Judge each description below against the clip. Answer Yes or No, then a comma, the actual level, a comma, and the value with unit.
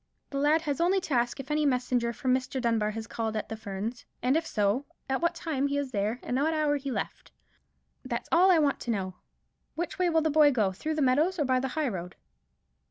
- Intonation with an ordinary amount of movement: Yes, average, 4.9 semitones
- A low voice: No, very high, 265 Hz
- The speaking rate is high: Yes, fast, 240 wpm